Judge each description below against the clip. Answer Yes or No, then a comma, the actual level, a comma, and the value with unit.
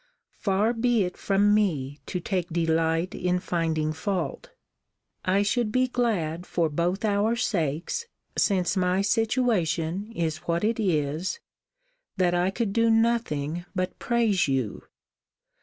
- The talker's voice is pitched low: No, medium, 185 Hz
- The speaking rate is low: Yes, slow, 130 wpm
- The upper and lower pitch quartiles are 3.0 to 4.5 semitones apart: No, average, 5.0 semitones